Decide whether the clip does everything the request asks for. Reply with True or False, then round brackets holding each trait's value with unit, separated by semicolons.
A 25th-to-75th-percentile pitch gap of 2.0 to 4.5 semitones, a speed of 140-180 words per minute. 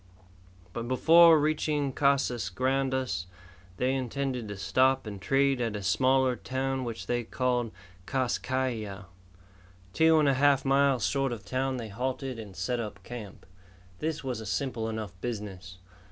True (3.5 semitones; 155 wpm)